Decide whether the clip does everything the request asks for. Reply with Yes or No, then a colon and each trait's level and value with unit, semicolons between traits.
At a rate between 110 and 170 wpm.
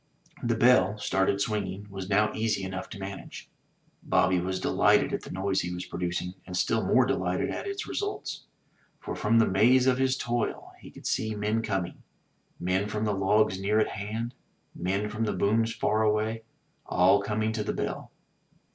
No: average, 185 wpm